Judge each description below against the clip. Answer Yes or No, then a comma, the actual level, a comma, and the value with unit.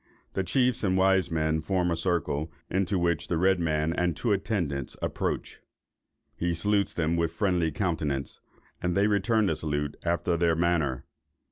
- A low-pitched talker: Yes, very low, 85 Hz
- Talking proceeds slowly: No, average, 160 wpm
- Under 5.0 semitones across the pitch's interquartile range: Yes, average, 3.2 semitones